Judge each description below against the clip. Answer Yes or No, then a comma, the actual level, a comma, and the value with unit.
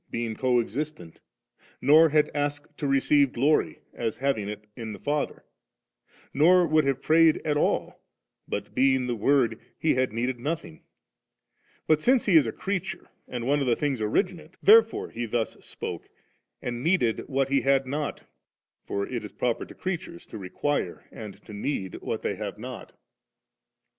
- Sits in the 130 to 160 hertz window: Yes, low, 135 Hz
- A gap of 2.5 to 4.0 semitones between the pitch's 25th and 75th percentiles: No, average, 4.5 semitones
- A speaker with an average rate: Yes, average, 165 wpm